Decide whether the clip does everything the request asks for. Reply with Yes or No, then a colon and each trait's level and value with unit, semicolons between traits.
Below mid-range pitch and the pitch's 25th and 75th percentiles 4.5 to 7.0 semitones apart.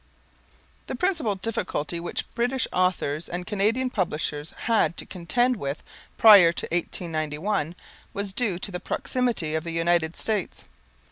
No: medium, 180 Hz; average, 5.1 semitones